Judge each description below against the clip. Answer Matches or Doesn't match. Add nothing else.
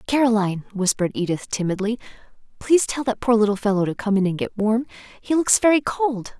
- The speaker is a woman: Matches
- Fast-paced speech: Doesn't match